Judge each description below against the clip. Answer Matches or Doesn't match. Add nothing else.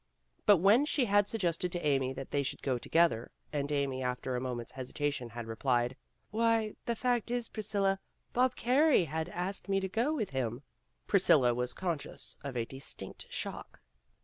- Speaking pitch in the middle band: Matches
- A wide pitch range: Matches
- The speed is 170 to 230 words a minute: Matches